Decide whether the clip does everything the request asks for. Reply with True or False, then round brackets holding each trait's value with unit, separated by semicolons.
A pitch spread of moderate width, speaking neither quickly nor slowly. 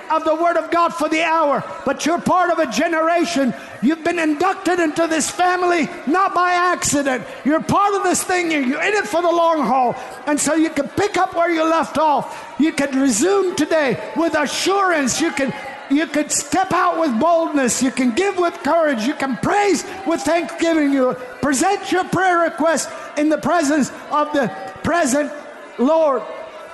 True (3.1 semitones; 185 wpm)